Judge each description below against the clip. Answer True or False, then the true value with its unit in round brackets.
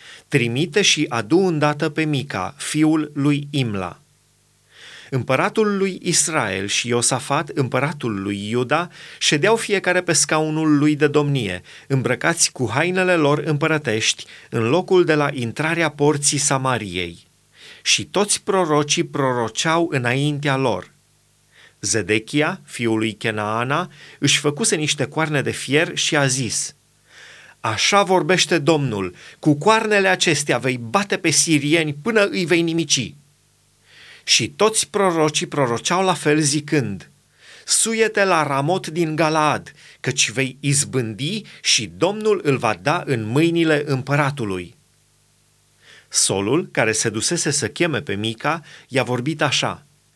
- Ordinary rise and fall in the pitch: True (4.7 semitones)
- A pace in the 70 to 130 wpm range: True (125 wpm)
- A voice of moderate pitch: True (150 Hz)